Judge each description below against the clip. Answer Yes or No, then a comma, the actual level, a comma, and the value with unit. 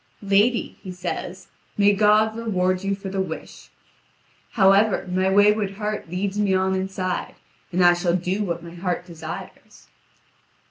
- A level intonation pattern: Yes, narrow, 2.1 semitones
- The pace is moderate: Yes, average, 145 wpm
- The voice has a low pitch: No, high, 190 Hz